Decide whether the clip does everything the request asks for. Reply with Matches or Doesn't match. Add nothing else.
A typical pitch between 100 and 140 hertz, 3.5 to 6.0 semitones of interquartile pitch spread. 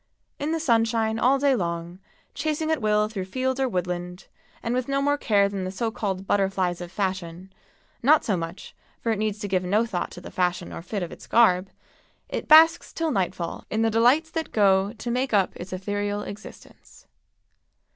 Doesn't match